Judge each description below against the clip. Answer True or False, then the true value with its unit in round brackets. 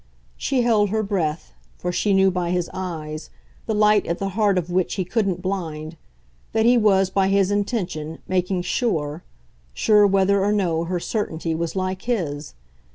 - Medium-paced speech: True (170 wpm)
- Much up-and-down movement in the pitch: False (3.4 semitones)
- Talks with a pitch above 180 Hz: True (190 Hz)